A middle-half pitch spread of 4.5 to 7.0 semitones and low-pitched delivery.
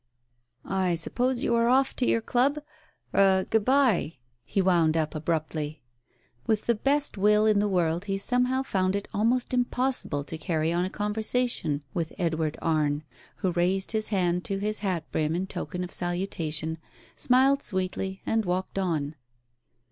No: average, 5.2 semitones; high, 190 Hz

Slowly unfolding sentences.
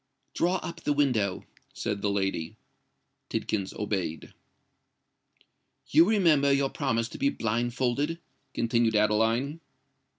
Yes: slow, 105 wpm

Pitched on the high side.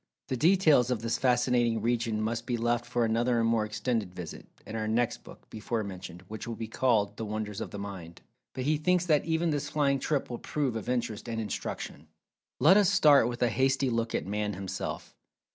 No: low, 120 Hz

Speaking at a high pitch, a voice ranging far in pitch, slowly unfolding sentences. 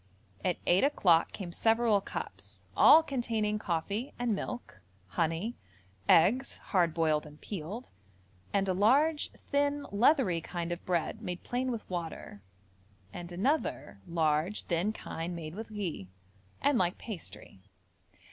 Yes: high, 195 Hz; wide, 5.8 semitones; slow, 130 wpm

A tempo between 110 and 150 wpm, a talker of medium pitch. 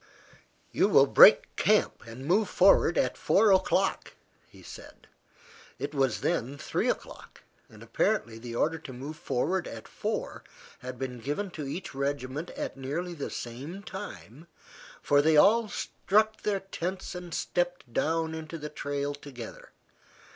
Yes: average, 145 wpm; medium, 150 Hz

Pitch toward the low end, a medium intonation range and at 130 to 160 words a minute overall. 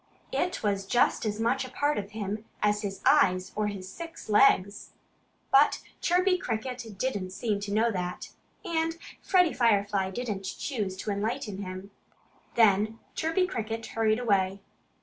No: high, 215 Hz; average, 4.0 semitones; average, 150 wpm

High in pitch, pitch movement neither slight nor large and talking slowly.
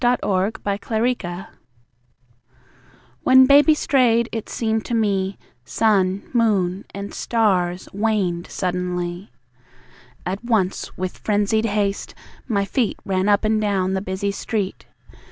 Yes: high, 200 Hz; average, 3.1 semitones; slow, 120 wpm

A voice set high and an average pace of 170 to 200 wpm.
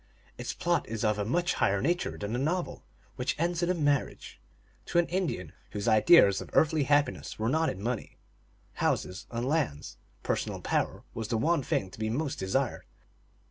No: low, 130 Hz; average, 180 wpm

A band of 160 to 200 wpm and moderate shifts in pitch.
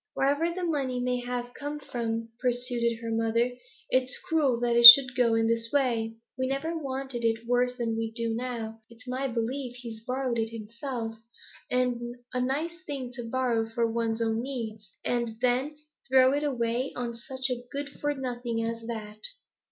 No: average, 175 wpm; narrow, 2.3 semitones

